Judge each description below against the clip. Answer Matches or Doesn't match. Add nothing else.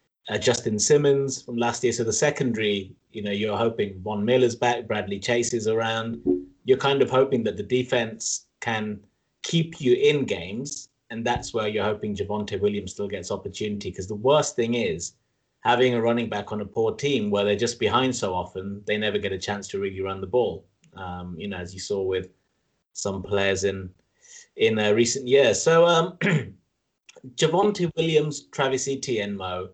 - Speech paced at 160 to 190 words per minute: Matches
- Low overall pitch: Matches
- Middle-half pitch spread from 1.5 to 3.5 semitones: Doesn't match